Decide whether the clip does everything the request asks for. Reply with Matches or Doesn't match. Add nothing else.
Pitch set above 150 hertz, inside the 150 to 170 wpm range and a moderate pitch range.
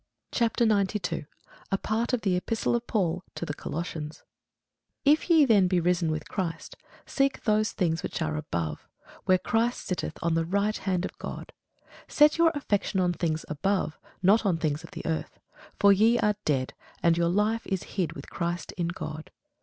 Doesn't match